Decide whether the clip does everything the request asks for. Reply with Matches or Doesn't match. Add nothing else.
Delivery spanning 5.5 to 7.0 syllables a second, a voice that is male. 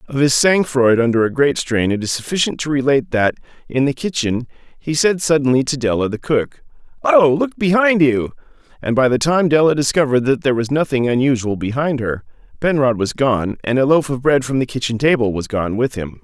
Matches